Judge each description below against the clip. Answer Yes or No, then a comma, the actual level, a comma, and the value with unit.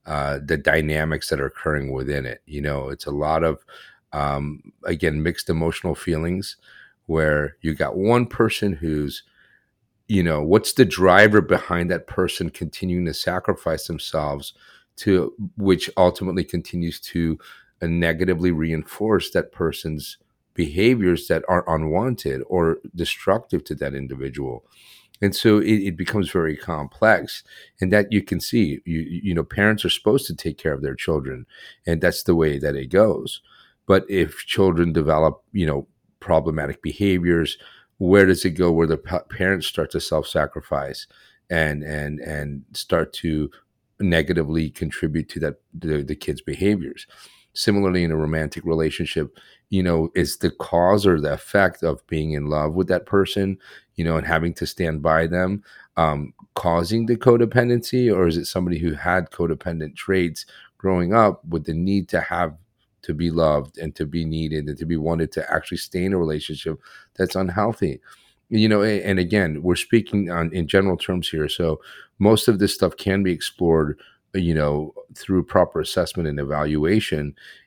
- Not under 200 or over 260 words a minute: No, average, 160 wpm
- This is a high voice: No, very low, 85 Hz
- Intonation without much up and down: No, average, 3.5 semitones